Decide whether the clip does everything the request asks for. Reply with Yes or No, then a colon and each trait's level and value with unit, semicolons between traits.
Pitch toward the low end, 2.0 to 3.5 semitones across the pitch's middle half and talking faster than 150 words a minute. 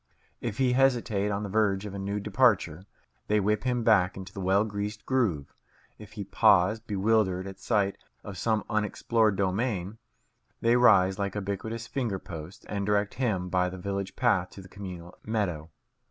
Yes: low, 100 Hz; average, 2.8 semitones; average, 170 wpm